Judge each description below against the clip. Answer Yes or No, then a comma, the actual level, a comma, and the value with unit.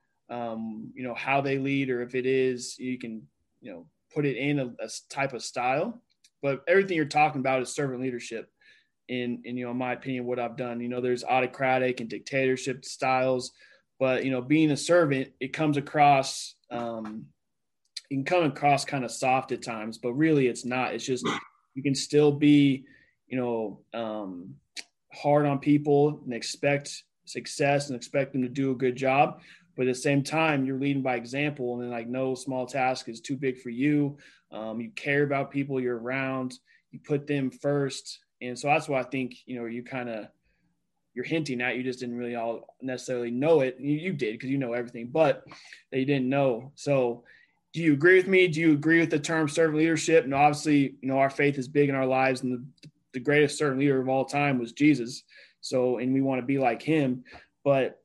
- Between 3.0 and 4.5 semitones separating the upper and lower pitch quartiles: No, narrow, 2.5 semitones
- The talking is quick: Yes, fast, 210 wpm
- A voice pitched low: Yes, low, 130 Hz